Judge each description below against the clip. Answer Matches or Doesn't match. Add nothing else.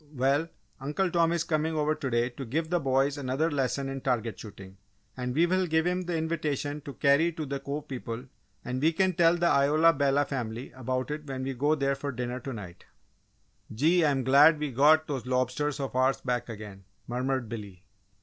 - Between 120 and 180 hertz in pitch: Matches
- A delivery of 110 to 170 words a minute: Doesn't match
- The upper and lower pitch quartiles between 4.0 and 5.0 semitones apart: Doesn't match